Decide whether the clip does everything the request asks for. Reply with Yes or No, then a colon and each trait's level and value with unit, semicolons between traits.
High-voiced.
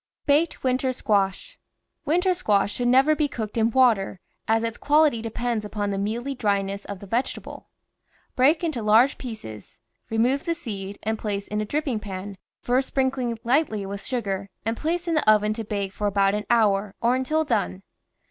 Yes: high, 225 Hz